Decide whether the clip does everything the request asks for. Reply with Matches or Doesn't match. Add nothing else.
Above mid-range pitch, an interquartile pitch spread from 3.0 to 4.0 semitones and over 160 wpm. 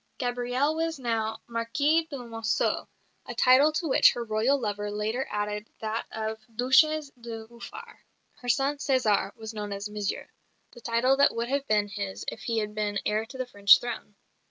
Matches